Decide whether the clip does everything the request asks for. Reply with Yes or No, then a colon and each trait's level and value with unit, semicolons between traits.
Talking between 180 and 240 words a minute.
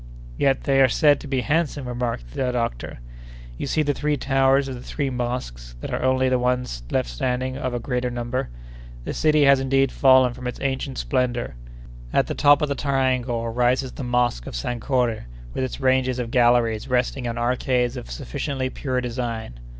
Yes: average, 185 wpm